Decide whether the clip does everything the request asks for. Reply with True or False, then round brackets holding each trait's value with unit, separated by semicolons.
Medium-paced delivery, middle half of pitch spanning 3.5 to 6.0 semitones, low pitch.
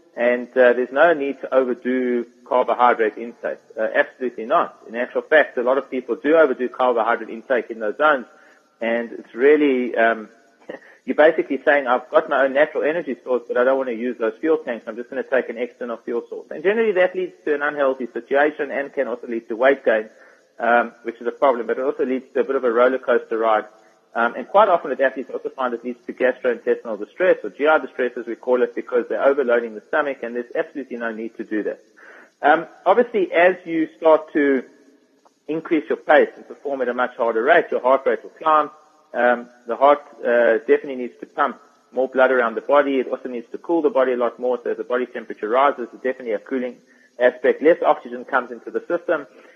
False (220 wpm; 5.1 semitones; 130 Hz)